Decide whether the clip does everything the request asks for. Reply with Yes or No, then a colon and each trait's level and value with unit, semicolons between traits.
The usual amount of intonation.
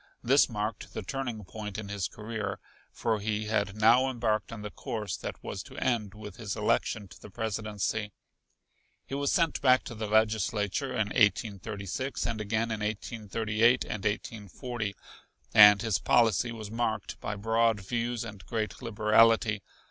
No: narrow, 1.9 semitones